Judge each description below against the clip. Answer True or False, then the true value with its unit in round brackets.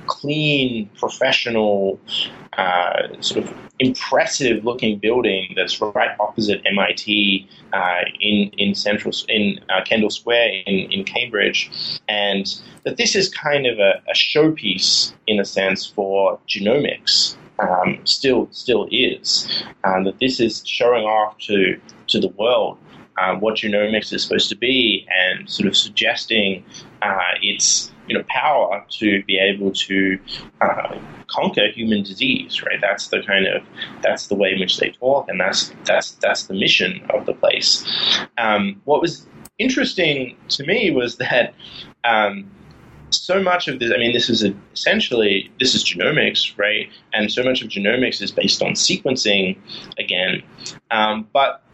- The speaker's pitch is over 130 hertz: False (110 Hz)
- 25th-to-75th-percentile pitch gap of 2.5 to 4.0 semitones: False (4.5 semitones)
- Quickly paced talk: False (150 wpm)